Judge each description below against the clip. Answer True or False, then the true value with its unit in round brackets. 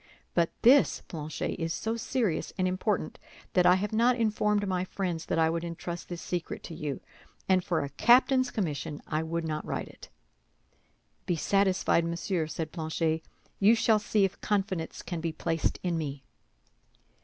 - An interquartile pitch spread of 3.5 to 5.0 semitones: True (4.1 semitones)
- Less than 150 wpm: False (165 wpm)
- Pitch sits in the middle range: True (175 Hz)